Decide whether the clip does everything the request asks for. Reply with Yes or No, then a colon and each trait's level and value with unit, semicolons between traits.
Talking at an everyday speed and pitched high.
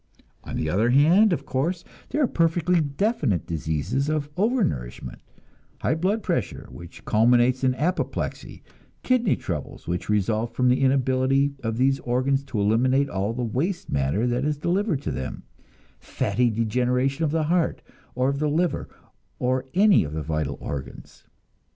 No: average, 155 wpm; low, 130 Hz